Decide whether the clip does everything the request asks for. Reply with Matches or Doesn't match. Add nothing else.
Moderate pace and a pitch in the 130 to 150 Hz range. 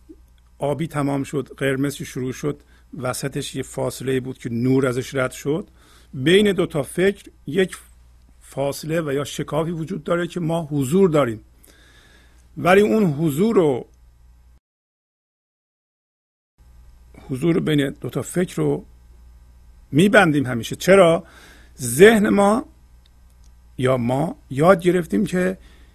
Matches